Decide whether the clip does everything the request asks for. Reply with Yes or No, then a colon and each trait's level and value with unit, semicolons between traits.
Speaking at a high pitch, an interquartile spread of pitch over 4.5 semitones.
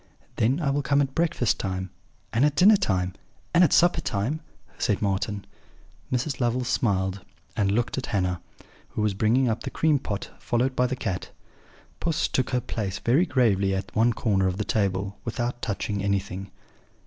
No: low, 115 Hz; average, 5.0 semitones